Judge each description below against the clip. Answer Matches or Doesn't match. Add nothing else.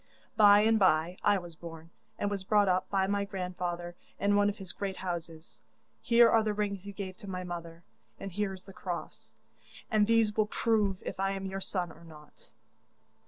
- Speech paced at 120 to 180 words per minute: Doesn't match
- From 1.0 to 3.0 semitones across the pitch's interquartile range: Matches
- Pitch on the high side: Matches